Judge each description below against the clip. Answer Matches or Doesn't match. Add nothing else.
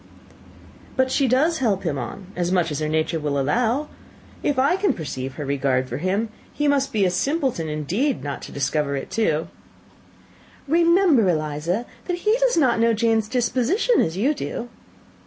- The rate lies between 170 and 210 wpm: Matches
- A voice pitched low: Doesn't match